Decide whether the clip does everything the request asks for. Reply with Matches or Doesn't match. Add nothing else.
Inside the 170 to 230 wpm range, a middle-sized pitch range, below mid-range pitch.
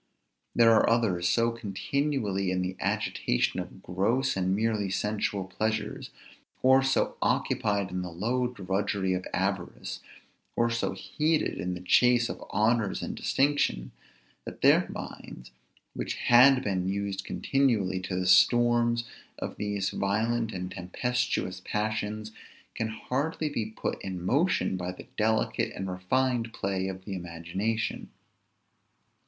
Doesn't match